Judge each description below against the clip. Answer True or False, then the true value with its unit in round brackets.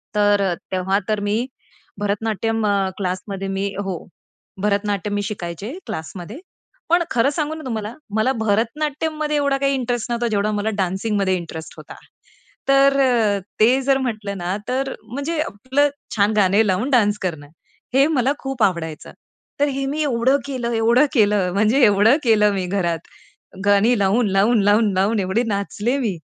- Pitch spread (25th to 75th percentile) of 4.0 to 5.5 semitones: True (4.6 semitones)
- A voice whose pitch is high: True (215 Hz)